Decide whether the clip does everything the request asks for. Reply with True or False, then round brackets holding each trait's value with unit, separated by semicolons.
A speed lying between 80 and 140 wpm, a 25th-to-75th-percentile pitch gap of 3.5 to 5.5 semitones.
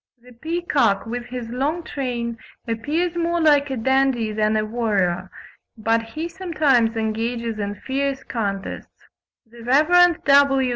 True (135 wpm; 4.4 semitones)